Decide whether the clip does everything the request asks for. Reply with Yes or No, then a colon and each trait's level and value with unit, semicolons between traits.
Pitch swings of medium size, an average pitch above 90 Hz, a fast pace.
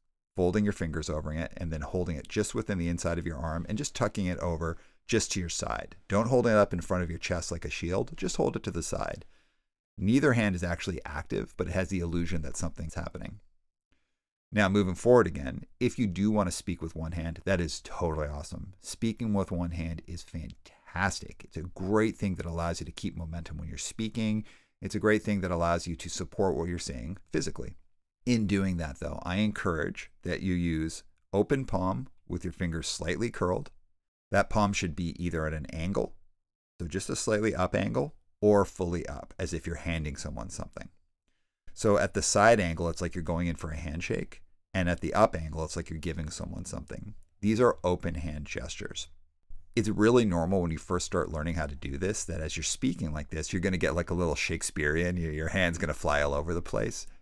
No: average, 3.1 semitones; very low, 85 Hz; fast, 215 wpm